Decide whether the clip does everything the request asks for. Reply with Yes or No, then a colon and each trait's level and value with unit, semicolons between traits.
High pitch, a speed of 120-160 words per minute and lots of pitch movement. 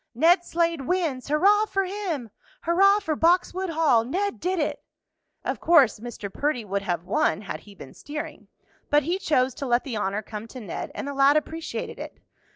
No: very high, 295 Hz; average, 185 wpm; wide, 6.9 semitones